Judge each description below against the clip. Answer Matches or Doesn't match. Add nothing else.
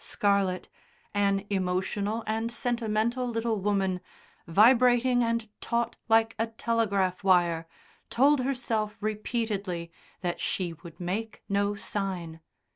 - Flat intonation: Doesn't match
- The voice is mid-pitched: Doesn't match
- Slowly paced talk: Matches